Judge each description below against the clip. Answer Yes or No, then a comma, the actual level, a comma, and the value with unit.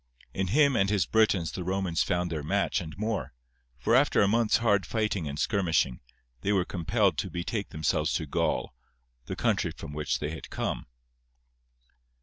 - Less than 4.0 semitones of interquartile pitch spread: No, average, 4.3 semitones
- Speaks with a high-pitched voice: No, very low, 95 Hz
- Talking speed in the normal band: Yes, average, 170 wpm